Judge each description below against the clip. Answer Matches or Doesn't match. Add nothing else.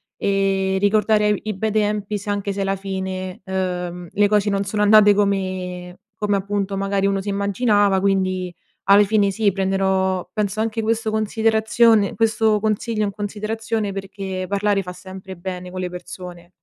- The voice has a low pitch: Doesn't match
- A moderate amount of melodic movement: Doesn't match